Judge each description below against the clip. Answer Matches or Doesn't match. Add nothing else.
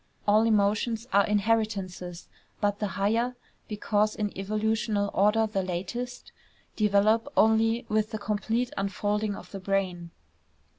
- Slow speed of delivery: Matches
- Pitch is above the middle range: Matches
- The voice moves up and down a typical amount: Doesn't match